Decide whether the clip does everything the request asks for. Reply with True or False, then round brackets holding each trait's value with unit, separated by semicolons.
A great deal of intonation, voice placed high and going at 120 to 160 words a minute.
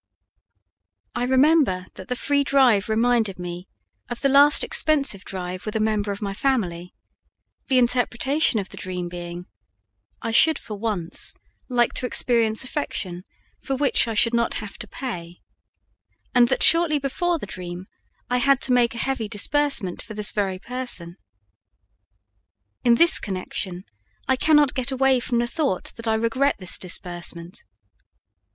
True (5.9 semitones; 230 Hz; 155 wpm)